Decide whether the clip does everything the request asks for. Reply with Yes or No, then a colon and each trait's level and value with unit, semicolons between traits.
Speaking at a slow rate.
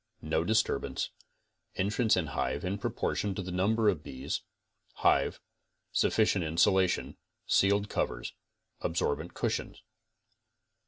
Yes: slow, 105 wpm